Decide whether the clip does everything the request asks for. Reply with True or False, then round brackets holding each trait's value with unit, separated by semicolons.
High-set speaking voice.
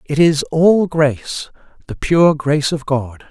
False (150 Hz)